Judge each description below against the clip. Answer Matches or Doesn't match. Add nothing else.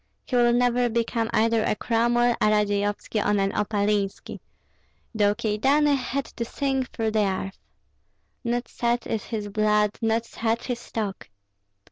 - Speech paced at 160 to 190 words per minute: Doesn't match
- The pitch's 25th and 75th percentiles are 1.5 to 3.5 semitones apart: Matches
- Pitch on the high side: Matches